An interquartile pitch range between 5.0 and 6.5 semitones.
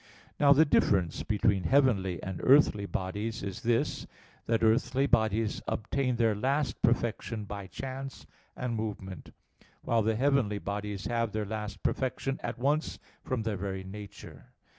No: average, 4.1 semitones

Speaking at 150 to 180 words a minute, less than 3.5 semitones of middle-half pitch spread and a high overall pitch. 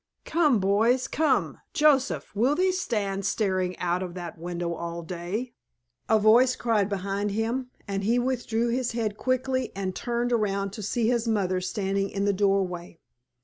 No: average, 155 wpm; average, 4.2 semitones; high, 210 Hz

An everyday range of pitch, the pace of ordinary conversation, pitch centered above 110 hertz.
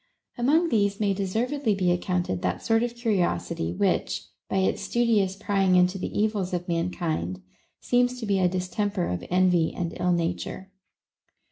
Yes: average, 3.6 semitones; average, 160 wpm; high, 190 Hz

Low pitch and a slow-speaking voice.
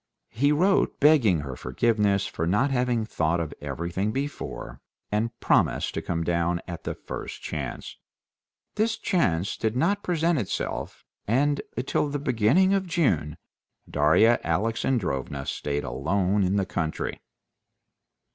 Yes: low, 105 Hz; slow, 130 wpm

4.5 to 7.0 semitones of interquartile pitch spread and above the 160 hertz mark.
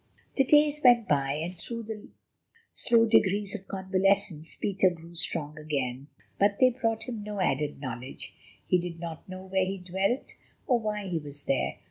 Yes: average, 5.1 semitones; high, 190 Hz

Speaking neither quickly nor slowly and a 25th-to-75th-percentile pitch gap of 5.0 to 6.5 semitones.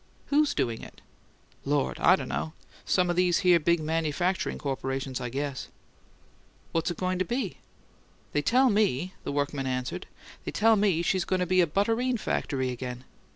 Yes: average, 170 wpm; wide, 5.5 semitones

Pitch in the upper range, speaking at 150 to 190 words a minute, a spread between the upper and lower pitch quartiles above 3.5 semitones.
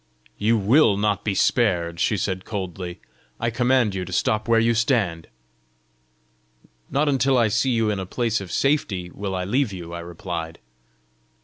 No: low, 105 Hz; average, 170 wpm; average, 4.3 semitones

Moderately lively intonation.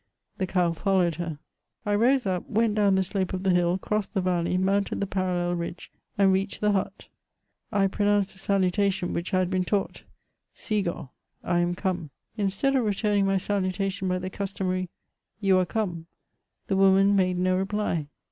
No: narrow, 1.7 semitones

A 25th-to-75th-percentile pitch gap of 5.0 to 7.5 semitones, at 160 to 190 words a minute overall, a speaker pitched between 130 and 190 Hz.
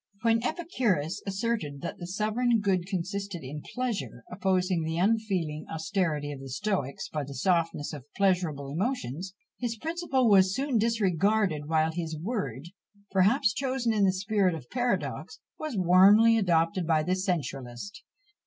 No: wide, 5.4 semitones; average, 145 wpm; medium, 185 Hz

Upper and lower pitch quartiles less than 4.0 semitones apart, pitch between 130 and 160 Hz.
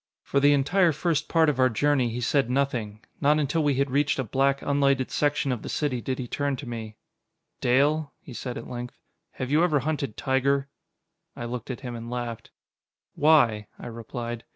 Yes: average, 3.0 semitones; low, 135 Hz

